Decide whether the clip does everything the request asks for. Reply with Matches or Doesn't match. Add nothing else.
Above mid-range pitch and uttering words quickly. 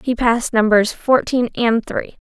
Doesn't match